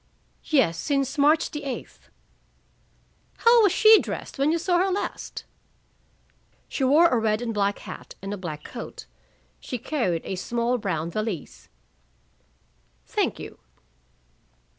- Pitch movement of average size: No, wide, 7.5 semitones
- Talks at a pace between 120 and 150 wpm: Yes, slow, 135 wpm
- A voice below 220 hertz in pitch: No, high, 245 Hz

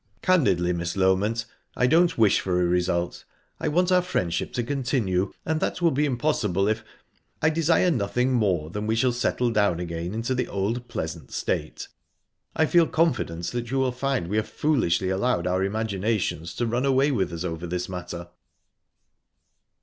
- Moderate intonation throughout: No, wide, 6.8 semitones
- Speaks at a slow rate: No, average, 175 wpm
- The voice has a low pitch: Yes, low, 110 Hz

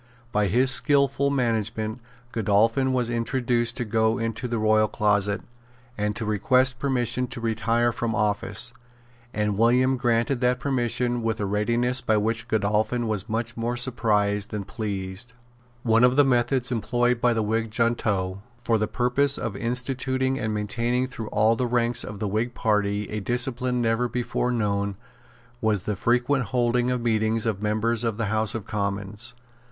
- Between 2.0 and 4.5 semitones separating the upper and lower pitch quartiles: Yes, narrow, 2.5 semitones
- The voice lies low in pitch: Yes, low, 115 Hz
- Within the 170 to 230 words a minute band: No, average, 160 wpm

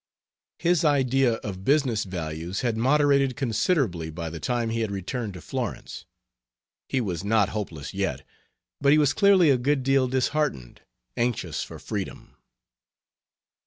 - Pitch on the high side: No, low, 120 Hz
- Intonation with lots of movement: Yes, wide, 6.3 semitones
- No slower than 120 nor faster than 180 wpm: Yes, average, 140 wpm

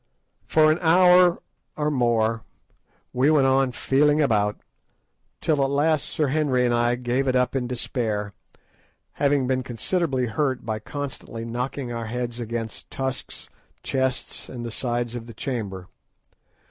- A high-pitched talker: No, low, 125 Hz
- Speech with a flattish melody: No, average, 3.3 semitones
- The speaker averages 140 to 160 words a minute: Yes, average, 145 wpm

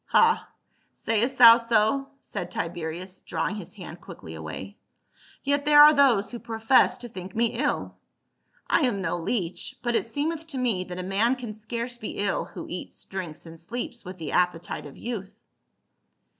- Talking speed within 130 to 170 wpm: No, average, 185 wpm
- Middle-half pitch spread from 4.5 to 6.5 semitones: Yes, wide, 5.4 semitones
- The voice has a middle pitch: No, high, 215 Hz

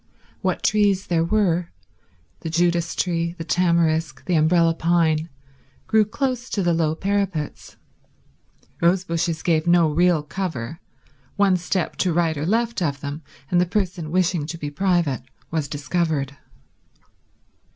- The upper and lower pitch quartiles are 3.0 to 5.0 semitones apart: No, narrow, 2.6 semitones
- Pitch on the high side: No, medium, 170 Hz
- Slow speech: Yes, slow, 130 wpm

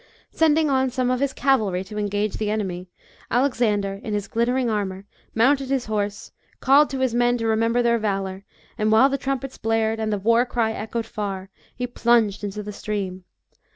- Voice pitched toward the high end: Yes, high, 225 Hz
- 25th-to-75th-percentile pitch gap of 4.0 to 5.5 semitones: No, average, 3.3 semitones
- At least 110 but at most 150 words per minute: No, average, 185 wpm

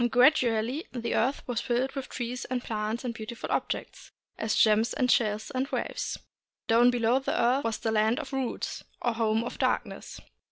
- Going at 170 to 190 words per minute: Yes, average, 175 wpm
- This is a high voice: Yes, high, 240 Hz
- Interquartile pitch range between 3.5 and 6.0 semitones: No, narrow, 2.6 semitones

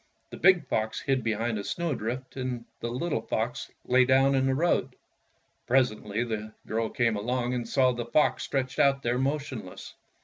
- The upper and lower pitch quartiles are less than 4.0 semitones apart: Yes, average, 2.8 semitones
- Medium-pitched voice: No, low, 125 Hz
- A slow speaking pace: No, average, 175 wpm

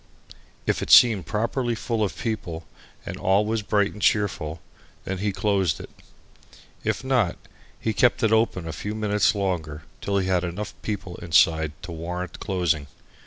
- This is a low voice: Yes, low, 100 Hz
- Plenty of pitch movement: No, average, 3.7 semitones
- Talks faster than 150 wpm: Yes, average, 165 wpm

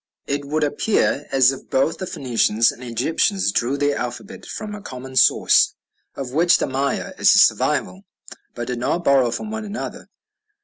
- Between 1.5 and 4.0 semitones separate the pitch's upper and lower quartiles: No, wide, 5.6 semitones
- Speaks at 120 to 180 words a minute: Yes, average, 175 wpm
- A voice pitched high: No, medium, 140 Hz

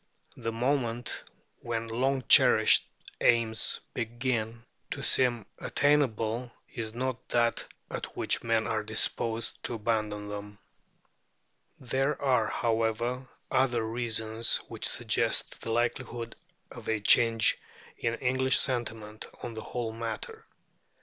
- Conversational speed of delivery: No, slow, 115 wpm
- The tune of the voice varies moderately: No, narrow, 1.9 semitones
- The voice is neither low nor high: No, low, 115 Hz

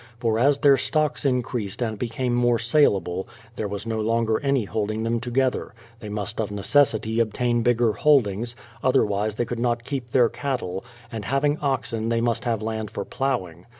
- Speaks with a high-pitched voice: No, low, 115 Hz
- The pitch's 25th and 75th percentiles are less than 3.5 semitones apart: Yes, average, 2.8 semitones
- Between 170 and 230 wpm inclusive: Yes, average, 180 wpm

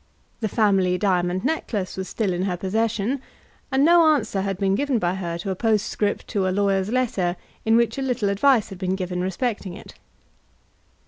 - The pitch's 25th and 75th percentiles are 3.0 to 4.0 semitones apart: Yes, average, 3.6 semitones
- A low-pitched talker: No, high, 200 Hz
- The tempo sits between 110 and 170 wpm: No, average, 185 wpm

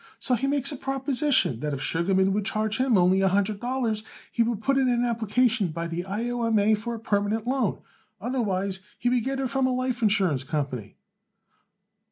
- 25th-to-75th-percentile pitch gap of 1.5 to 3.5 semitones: No, average, 4.8 semitones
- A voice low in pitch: No, high, 220 Hz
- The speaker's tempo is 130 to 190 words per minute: No, fast, 205 wpm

